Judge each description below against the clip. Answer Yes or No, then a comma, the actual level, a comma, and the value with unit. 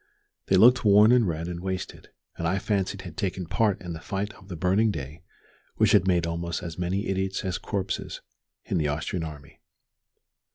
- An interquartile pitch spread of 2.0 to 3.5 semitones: Yes, average, 2.9 semitones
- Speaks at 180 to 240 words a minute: Yes, average, 190 wpm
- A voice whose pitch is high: No, very low, 95 Hz